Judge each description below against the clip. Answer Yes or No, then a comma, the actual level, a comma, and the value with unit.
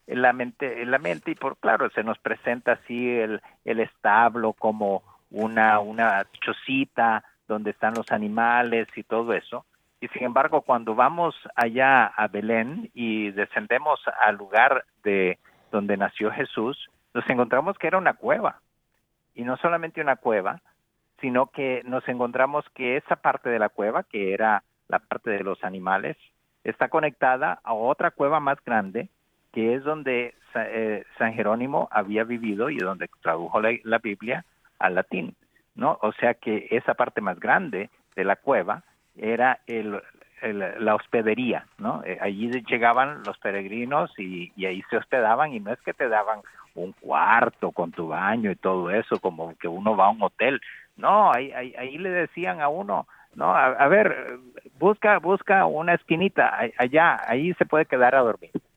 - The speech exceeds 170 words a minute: No, average, 165 wpm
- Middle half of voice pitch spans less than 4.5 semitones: Yes, average, 3.6 semitones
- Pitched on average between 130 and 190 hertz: No, low, 115 Hz